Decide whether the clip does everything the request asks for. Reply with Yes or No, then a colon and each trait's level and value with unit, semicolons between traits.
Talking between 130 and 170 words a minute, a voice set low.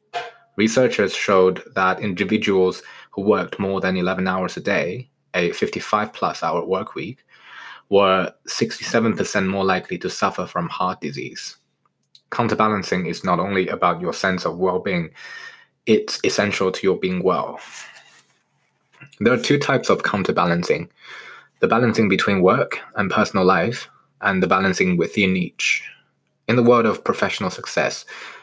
Yes: average, 140 wpm; low, 110 Hz